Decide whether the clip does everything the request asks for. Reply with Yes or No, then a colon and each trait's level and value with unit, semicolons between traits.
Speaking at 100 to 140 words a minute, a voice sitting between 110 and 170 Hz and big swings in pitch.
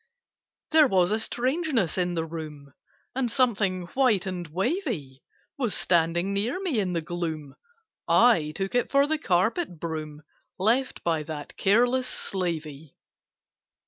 No: slow, 135 wpm; medium, 185 Hz; wide, 7.2 semitones